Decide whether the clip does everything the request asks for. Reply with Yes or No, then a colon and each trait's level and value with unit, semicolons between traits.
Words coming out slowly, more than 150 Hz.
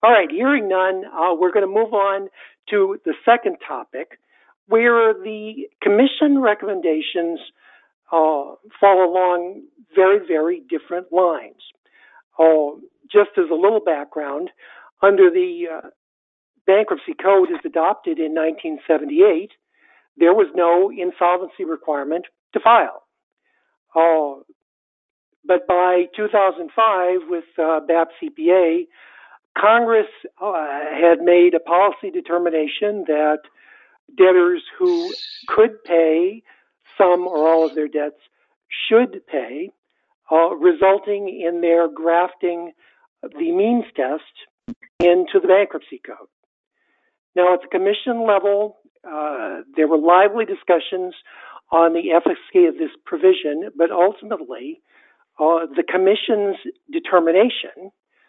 Yes: slow, 110 wpm; high, 190 Hz